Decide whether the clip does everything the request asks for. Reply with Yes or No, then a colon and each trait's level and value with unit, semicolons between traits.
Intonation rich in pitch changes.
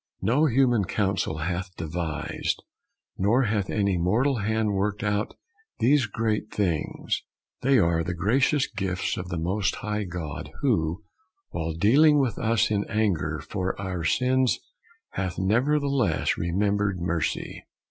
No: average, 4.4 semitones